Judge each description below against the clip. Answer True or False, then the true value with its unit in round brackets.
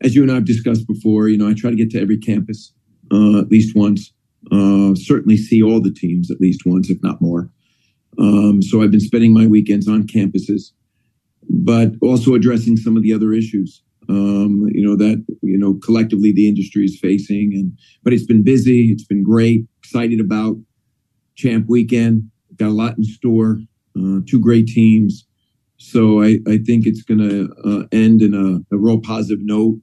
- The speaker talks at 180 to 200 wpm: True (190 wpm)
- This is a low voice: True (110 Hz)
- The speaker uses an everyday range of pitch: False (1.8 semitones)